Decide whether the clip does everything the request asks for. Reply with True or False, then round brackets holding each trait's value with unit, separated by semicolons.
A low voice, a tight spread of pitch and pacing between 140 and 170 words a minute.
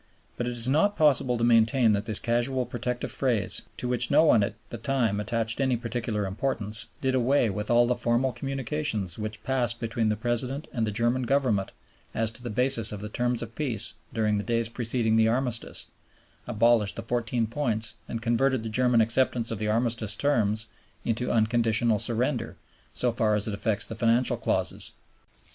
False (115 Hz; 2.2 semitones; 185 wpm)